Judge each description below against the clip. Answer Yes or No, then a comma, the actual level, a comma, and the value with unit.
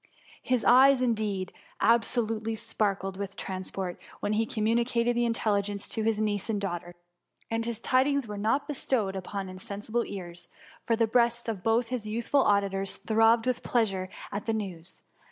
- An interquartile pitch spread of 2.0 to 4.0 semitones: Yes, average, 3.0 semitones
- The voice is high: Yes, high, 220 Hz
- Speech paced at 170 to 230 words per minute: No, average, 155 wpm